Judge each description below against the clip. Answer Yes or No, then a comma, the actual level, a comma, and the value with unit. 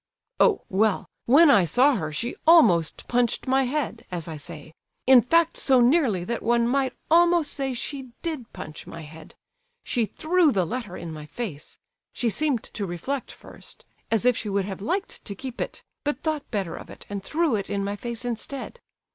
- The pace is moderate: Yes, average, 190 wpm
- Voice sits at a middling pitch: No, high, 240 Hz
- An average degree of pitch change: No, wide, 6.4 semitones